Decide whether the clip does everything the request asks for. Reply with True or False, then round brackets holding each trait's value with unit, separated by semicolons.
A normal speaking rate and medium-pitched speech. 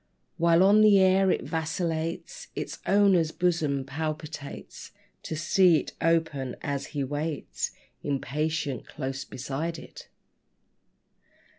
False (110 wpm; 160 Hz)